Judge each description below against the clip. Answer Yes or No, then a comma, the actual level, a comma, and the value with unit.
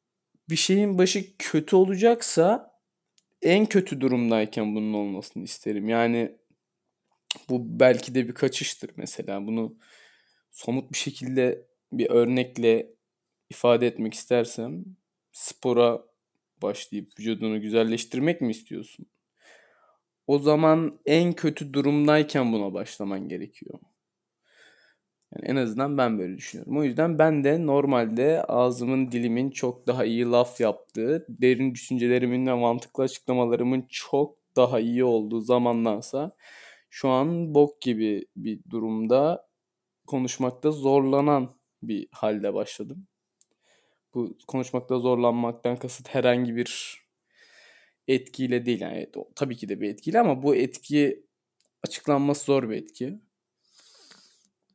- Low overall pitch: Yes, low, 125 Hz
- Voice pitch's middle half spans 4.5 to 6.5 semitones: No, average, 3.6 semitones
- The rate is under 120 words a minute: Yes, average, 110 wpm